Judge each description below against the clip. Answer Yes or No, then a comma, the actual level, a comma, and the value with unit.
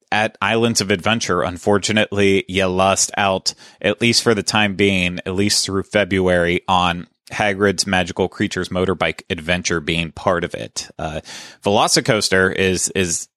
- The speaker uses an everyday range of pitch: No, narrow, 2.3 semitones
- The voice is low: Yes, very low, 95 Hz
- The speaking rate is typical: Yes, average, 145 wpm